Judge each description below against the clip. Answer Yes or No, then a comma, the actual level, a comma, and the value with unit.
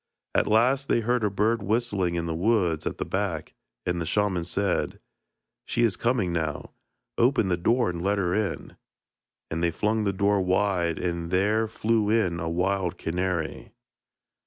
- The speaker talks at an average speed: Yes, average, 170 wpm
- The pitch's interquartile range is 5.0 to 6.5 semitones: No, average, 4.0 semitones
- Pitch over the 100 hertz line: No, very low, 95 Hz